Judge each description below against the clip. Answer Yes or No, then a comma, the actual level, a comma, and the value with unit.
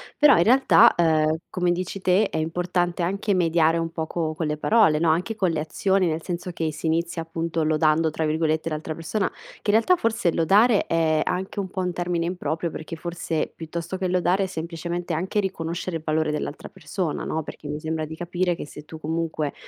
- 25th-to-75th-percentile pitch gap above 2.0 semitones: Yes, narrow, 2.5 semitones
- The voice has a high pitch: No, medium, 170 Hz